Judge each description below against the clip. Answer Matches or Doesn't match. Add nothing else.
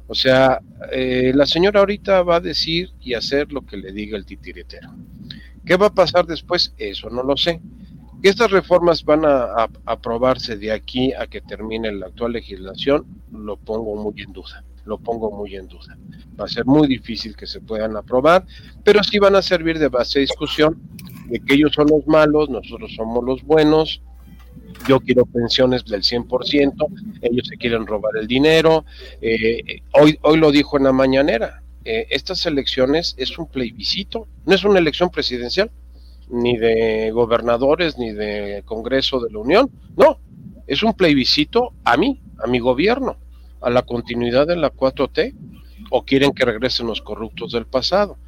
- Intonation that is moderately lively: Doesn't match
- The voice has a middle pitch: Doesn't match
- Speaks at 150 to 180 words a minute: Matches